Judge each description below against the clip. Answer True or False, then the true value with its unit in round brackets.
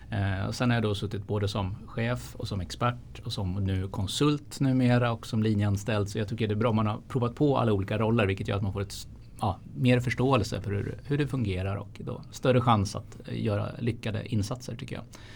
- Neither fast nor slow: False (225 wpm)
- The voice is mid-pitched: False (110 Hz)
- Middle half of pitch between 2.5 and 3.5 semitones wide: True (3.2 semitones)